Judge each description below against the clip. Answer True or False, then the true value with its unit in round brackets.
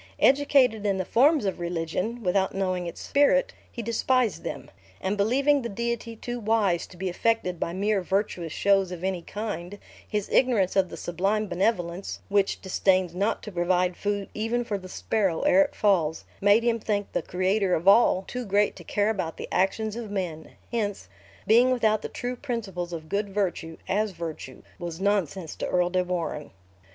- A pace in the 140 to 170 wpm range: False (180 wpm)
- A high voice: True (200 Hz)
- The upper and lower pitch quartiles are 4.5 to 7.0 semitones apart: False (3.9 semitones)